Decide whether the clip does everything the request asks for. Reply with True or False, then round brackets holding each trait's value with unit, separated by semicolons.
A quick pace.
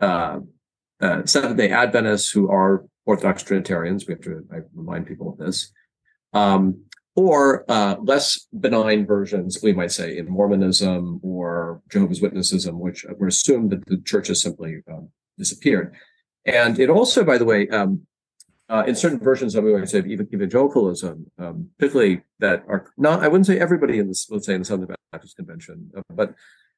False (170 wpm)